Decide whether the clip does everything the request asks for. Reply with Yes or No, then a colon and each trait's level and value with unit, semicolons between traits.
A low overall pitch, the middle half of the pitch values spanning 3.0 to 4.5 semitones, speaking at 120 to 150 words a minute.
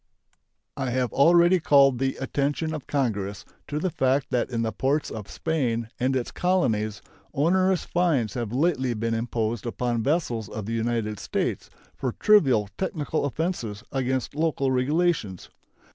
No: low, 130 Hz; average, 5.2 semitones; average, 145 wpm